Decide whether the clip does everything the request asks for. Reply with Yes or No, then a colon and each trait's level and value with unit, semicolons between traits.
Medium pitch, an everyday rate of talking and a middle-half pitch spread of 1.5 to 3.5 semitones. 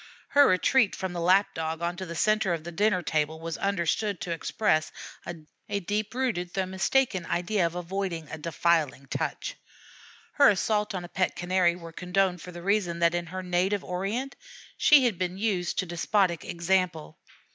Yes: medium, 180 Hz; average, 175 wpm; average, 2.9 semitones